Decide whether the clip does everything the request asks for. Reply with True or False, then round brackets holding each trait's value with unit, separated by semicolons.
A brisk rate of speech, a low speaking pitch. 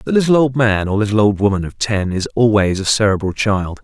True (235 wpm; 105 Hz)